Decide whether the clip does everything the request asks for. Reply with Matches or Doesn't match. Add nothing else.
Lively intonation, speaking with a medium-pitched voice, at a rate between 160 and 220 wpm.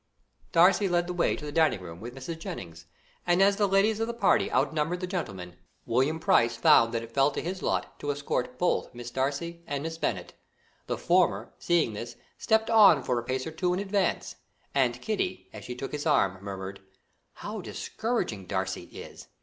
Matches